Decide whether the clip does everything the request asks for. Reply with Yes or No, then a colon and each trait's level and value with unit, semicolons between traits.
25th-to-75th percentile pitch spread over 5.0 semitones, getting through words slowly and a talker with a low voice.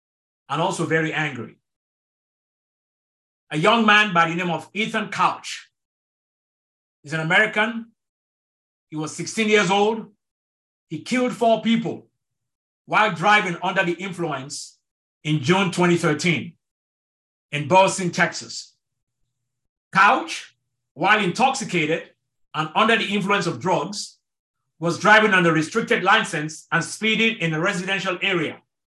No: wide, 5.4 semitones; slow, 115 wpm; medium, 175 Hz